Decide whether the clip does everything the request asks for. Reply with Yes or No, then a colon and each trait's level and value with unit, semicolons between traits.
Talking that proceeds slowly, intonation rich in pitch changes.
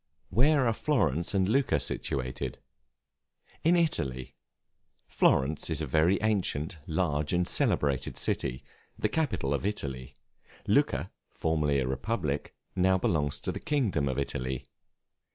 Yes: slow, 125 wpm; wide, 7.2 semitones